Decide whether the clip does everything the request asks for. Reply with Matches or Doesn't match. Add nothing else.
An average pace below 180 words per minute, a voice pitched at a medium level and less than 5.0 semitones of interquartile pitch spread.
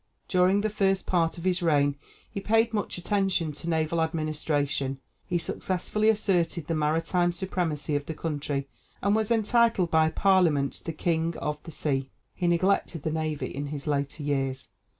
Matches